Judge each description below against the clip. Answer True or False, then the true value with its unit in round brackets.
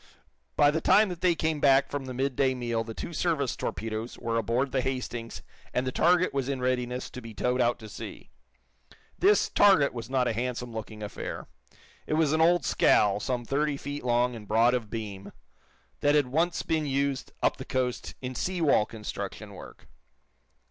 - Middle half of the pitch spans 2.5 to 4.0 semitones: True (3.7 semitones)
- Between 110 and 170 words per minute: False (190 wpm)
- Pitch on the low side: True (130 Hz)